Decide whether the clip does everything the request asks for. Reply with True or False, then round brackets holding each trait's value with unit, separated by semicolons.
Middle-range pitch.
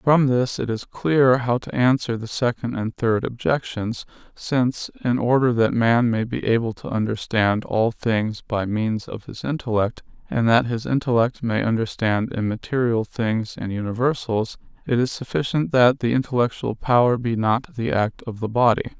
False (120 Hz)